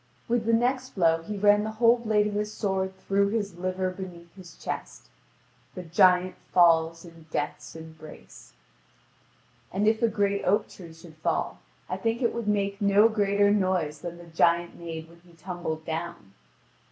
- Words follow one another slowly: No, average, 170 wpm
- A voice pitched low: No, medium, 185 Hz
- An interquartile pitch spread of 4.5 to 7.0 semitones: No, average, 3.6 semitones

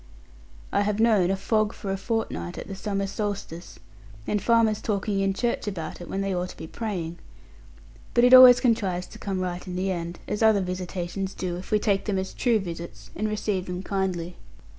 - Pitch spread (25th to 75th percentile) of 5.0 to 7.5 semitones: No, average, 2.9 semitones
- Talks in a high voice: Yes, high, 195 Hz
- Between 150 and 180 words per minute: No, fast, 205 wpm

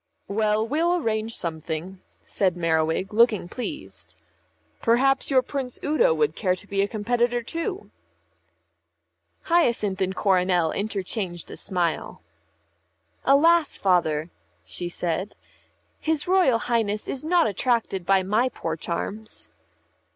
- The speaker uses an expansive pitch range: Yes, wide, 5.9 semitones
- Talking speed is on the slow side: Yes, slow, 115 wpm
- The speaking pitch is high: Yes, high, 210 Hz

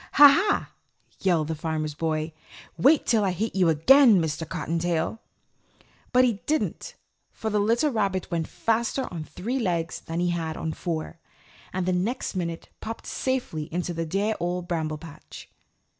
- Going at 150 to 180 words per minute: Yes, average, 160 wpm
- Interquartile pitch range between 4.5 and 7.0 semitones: Yes, wide, 5.4 semitones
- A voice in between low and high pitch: Yes, medium, 180 Hz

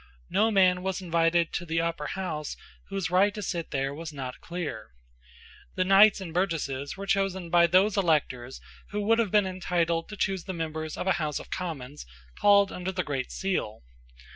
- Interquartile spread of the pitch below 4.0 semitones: Yes, average, 3.5 semitones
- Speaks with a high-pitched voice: No, medium, 175 Hz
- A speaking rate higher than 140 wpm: Yes, average, 185 wpm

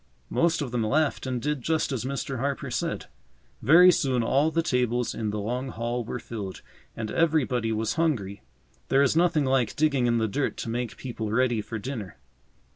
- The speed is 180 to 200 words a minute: Yes, average, 190 wpm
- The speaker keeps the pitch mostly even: No, average, 4.0 semitones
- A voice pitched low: Yes, low, 125 Hz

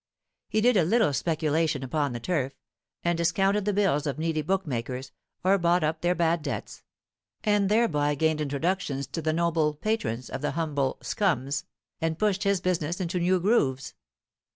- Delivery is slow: No, average, 165 wpm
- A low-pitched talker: No, medium, 165 Hz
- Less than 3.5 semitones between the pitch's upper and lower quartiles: No, average, 4.2 semitones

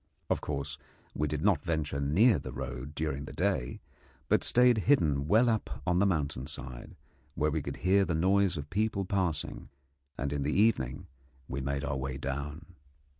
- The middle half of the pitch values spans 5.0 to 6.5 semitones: Yes, wide, 5.6 semitones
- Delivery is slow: No, average, 175 wpm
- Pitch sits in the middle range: No, very low, 75 Hz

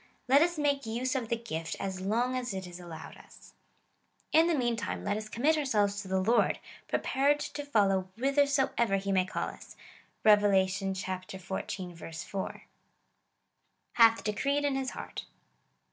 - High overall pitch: Yes, high, 220 Hz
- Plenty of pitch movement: Yes, wide, 6.0 semitones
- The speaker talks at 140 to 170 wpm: Yes, average, 150 wpm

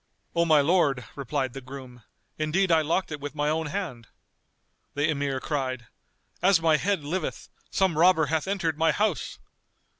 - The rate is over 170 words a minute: No, average, 160 wpm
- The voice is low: No, medium, 155 Hz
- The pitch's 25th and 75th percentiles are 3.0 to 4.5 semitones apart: Yes, average, 3.4 semitones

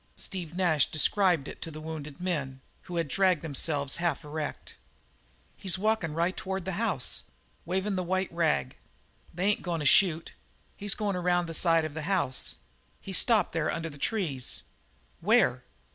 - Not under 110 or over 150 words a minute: No, average, 165 wpm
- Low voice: No, medium, 170 Hz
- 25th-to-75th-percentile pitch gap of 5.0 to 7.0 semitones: No, average, 3.5 semitones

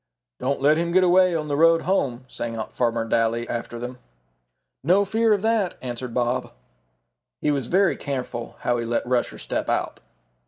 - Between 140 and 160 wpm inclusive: No, average, 180 wpm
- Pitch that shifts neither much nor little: No, wide, 6.6 semitones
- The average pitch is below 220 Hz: Yes, low, 135 Hz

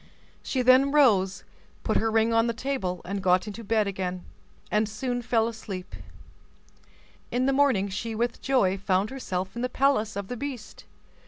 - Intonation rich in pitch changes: No, average, 4.5 semitones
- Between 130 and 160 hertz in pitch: No, high, 225 Hz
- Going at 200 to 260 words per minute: No, average, 165 wpm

